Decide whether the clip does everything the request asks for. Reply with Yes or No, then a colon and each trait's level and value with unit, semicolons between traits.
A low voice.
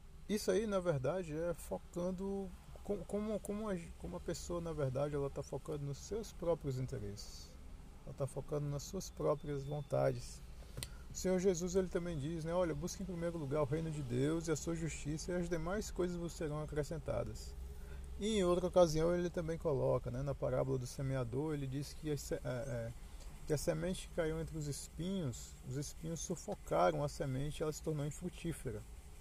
No: medium, 155 Hz